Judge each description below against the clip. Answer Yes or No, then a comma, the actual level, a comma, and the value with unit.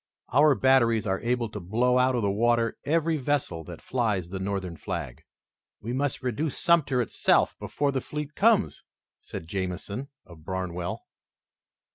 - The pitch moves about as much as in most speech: No, wide, 6.3 semitones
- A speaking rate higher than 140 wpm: Yes, average, 150 wpm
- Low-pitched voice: Yes, low, 120 Hz